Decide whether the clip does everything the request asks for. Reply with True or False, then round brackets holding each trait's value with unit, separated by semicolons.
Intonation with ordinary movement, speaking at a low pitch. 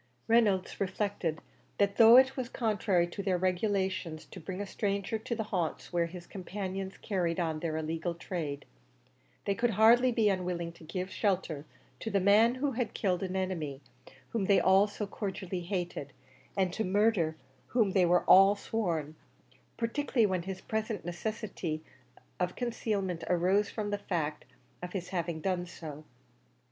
False (3.4 semitones; 190 Hz)